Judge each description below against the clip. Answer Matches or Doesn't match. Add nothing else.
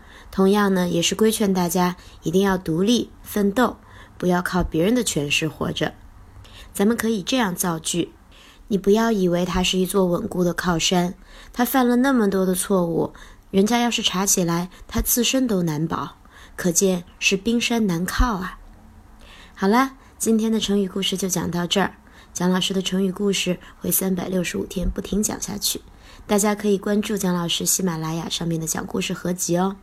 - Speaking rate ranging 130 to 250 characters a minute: Doesn't match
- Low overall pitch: Doesn't match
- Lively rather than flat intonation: Doesn't match